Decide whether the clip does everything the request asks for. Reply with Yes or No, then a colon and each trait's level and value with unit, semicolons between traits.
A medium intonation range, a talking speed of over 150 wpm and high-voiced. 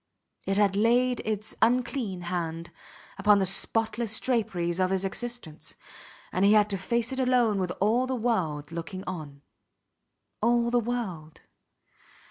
No: average, 4.6 semitones; average, 140 wpm; high, 210 Hz